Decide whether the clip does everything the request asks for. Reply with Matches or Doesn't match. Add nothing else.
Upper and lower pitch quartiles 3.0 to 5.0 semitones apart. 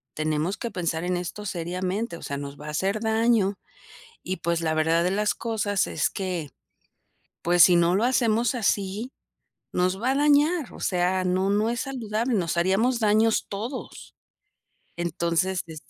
Matches